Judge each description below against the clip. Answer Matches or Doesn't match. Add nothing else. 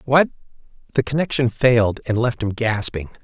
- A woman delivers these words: Doesn't match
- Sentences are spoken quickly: Doesn't match